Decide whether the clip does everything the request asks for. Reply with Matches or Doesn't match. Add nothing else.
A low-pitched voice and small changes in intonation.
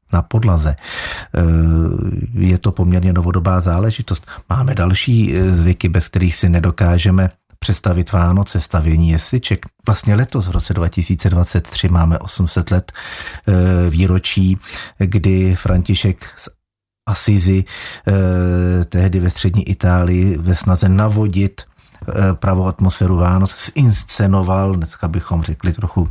Matches